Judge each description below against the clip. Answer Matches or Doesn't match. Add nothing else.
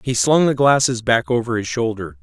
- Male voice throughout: Matches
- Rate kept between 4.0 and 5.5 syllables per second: Matches